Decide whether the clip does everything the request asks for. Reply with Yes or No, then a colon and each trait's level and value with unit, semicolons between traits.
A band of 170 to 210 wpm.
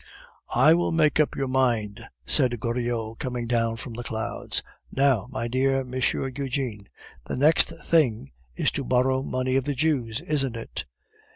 No: average, 160 wpm